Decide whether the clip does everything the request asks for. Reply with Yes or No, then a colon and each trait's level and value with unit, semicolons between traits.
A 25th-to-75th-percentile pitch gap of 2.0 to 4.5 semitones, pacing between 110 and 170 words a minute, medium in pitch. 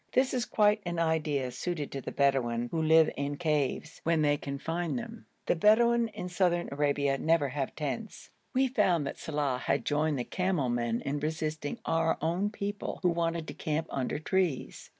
No: average, 4.2 semitones; average, 185 wpm; medium, 160 Hz